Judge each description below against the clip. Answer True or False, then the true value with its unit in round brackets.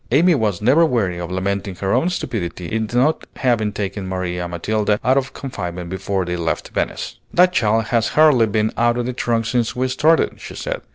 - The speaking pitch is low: True (110 Hz)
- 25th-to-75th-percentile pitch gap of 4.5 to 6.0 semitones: True (5.2 semitones)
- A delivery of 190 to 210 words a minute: True (195 wpm)